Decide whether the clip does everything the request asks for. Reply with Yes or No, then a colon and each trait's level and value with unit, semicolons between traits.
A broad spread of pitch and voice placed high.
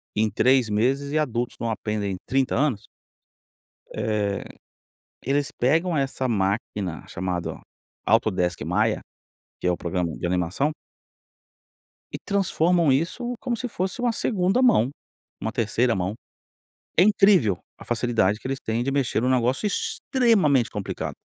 No: wide, 7.6 semitones; low, 125 Hz